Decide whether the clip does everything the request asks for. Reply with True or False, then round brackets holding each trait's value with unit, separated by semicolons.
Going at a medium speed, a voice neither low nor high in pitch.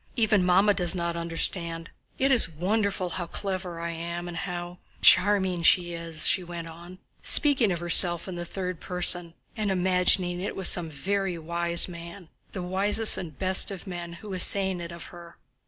True (170 wpm; 180 Hz)